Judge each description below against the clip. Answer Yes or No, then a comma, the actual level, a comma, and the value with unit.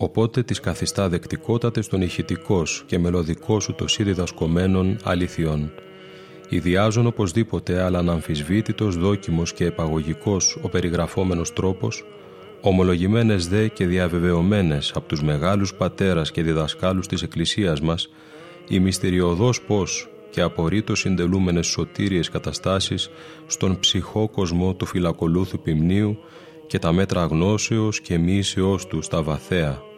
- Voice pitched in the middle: No, very low, 95 Hz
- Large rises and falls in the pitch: No, average, 3.5 semitones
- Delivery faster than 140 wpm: No, average, 120 wpm